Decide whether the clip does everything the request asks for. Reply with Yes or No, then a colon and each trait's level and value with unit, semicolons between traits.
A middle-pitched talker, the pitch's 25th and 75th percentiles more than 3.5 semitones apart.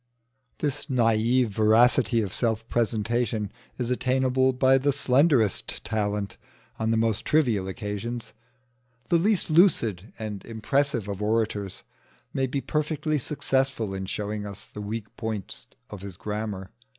No: low, 115 Hz; average, 3.9 semitones